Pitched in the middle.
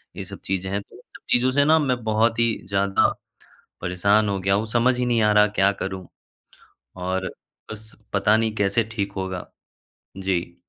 No: low, 105 Hz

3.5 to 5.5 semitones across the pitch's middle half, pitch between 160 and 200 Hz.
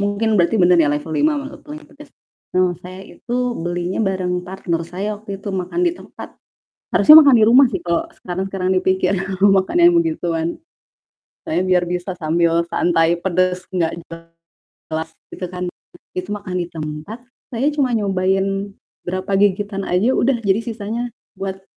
Yes: average, 3.9 semitones; high, 190 Hz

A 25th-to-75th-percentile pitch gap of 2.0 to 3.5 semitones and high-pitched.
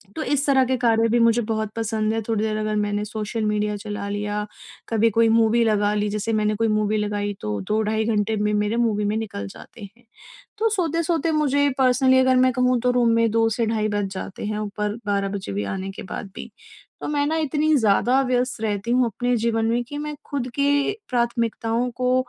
Yes: average, 3.1 semitones; high, 225 Hz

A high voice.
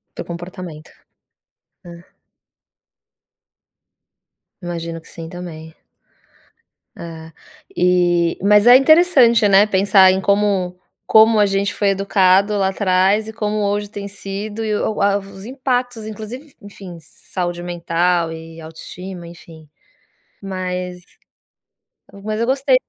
Yes: high, 195 Hz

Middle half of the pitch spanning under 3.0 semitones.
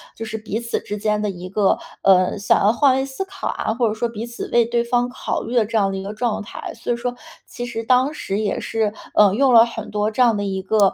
Yes: narrow, 2.5 semitones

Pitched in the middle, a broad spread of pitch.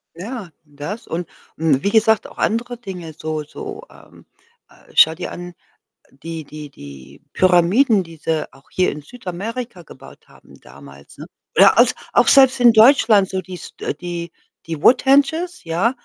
Yes: medium, 180 Hz; wide, 6.6 semitones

